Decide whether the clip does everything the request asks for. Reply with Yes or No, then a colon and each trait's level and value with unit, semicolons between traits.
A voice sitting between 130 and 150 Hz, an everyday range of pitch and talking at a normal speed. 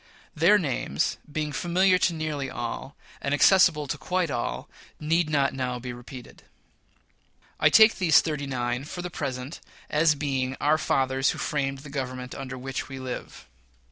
Yes: medium, 140 Hz; average, 3.4 semitones; average, 160 wpm